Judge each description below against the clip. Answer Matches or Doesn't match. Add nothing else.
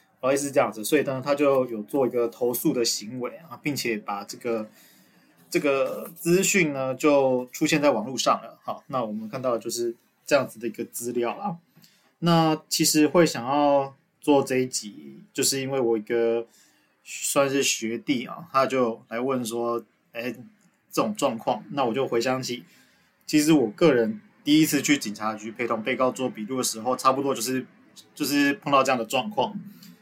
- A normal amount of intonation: Matches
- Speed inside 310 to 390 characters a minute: Doesn't match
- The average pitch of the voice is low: Matches